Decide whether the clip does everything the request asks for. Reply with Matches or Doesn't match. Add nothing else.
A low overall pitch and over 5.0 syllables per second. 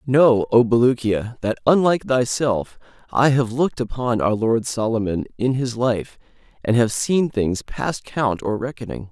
Doesn't match